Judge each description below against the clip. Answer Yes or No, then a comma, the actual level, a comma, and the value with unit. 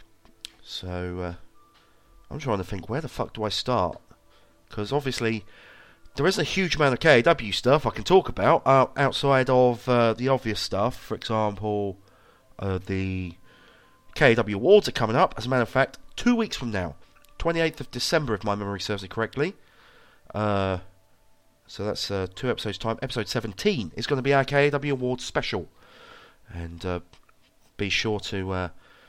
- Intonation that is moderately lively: No, wide, 5.7 semitones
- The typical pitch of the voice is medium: No, low, 115 Hz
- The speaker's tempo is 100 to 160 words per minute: No, average, 170 wpm